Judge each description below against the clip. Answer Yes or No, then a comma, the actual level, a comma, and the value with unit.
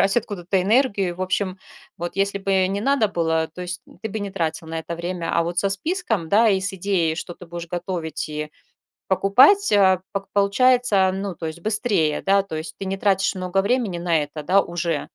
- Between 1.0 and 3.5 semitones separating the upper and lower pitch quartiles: Yes, average, 2.8 semitones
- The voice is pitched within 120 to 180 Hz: No, high, 190 Hz